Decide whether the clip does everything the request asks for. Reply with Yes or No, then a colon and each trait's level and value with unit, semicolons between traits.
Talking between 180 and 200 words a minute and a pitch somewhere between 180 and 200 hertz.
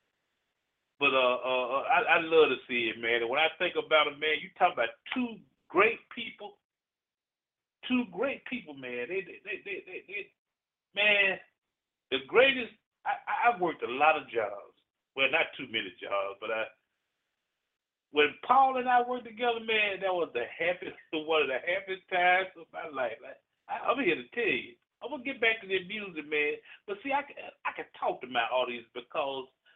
Yes: average, 190 wpm; high, 190 Hz